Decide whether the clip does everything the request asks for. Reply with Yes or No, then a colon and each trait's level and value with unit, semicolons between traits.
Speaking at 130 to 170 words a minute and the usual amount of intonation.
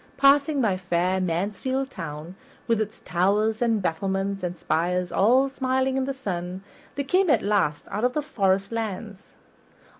No: average, 155 wpm; wide, 6.0 semitones